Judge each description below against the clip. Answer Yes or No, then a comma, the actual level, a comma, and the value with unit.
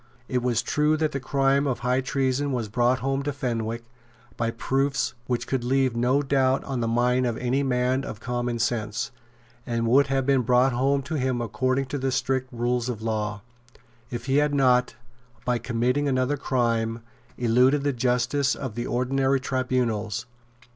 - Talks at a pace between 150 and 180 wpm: Yes, average, 175 wpm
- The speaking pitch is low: Yes, low, 125 Hz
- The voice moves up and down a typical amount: No, narrow, 2.2 semitones